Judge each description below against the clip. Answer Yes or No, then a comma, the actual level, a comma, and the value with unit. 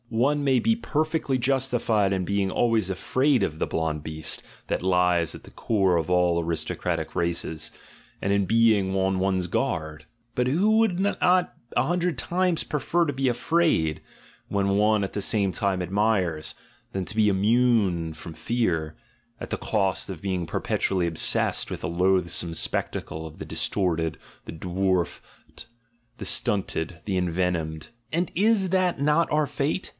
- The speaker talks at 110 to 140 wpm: No, average, 160 wpm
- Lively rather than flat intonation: Yes, wide, 7.3 semitones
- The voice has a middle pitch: No, very low, 95 Hz